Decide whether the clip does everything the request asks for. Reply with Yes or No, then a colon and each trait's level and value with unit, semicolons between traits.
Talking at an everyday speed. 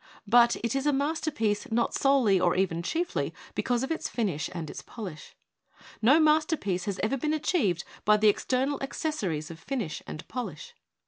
Yes: average, 170 wpm